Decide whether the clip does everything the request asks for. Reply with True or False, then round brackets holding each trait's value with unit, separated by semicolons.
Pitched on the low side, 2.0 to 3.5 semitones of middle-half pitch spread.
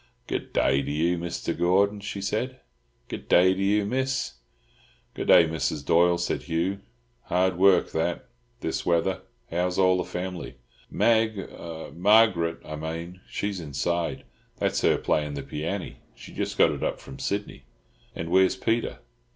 True (90 Hz; 3.2 semitones)